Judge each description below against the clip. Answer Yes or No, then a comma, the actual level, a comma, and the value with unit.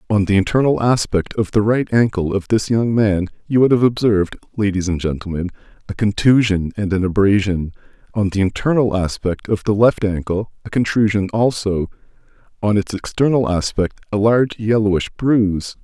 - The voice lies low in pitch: Yes, low, 105 Hz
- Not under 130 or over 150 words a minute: No, average, 165 wpm